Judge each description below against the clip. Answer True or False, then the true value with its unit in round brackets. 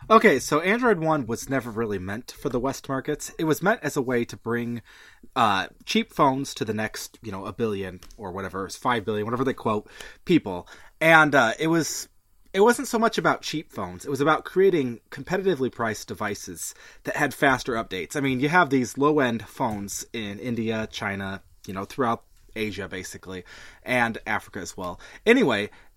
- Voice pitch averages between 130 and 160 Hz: False (120 Hz)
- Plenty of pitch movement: True (6.3 semitones)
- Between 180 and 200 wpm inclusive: True (185 wpm)